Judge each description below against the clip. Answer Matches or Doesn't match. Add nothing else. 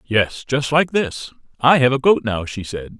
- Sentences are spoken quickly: Matches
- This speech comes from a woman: Doesn't match